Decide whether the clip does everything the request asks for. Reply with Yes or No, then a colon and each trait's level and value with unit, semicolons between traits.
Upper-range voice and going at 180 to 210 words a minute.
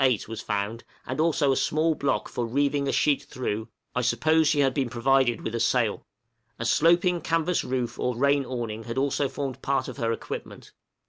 No: low, 135 Hz; average, 195 wpm